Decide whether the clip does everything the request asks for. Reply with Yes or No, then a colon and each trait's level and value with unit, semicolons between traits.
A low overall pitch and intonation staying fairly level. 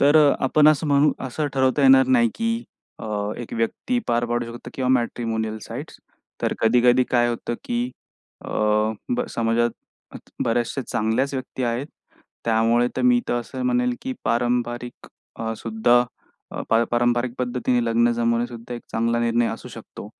Yes: low, 120 Hz; narrow, 2.0 semitones